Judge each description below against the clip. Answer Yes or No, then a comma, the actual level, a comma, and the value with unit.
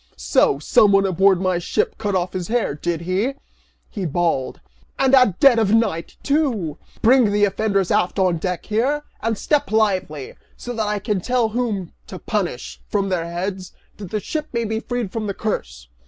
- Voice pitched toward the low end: No, high, 205 Hz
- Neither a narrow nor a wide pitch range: Yes, average, 3.8 semitones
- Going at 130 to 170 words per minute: No, average, 185 wpm